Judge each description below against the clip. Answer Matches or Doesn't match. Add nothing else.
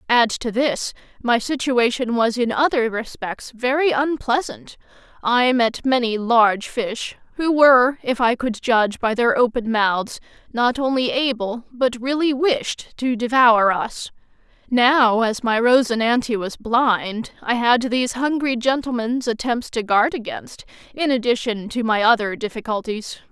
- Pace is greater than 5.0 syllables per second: Doesn't match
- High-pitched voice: Matches